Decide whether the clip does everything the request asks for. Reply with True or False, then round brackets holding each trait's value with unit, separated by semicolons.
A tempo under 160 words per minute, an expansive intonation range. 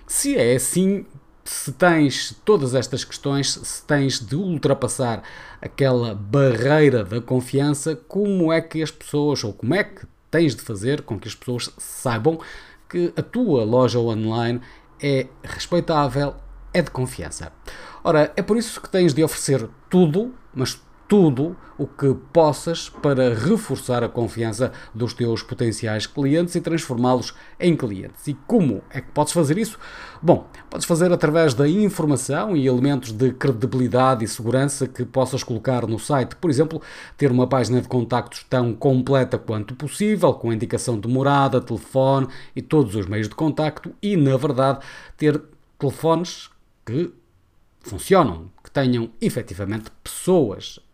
False (150 wpm; 4.2 semitones)